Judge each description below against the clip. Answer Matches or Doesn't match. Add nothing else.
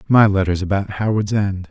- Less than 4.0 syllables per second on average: Doesn't match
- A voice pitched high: Doesn't match